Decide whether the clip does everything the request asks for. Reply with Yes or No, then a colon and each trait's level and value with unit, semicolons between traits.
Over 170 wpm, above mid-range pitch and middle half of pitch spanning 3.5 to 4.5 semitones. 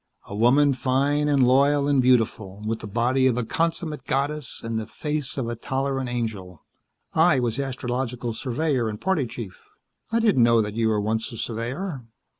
No: average, 180 wpm; low, 125 Hz; average, 3.8 semitones